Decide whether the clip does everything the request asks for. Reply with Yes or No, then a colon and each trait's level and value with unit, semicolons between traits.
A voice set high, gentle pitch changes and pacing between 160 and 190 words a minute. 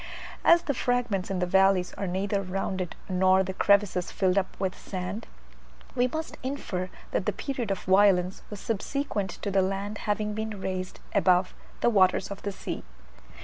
Yes: high, 195 Hz; narrow, 2.1 semitones; average, 170 wpm